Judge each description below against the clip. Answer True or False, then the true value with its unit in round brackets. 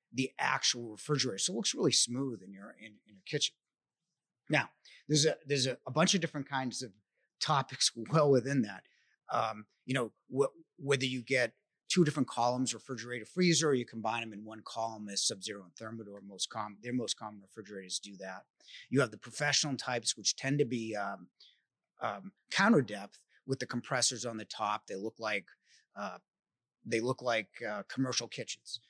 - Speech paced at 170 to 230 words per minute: True (185 wpm)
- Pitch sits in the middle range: False (120 Hz)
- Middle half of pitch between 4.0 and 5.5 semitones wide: False (3.6 semitones)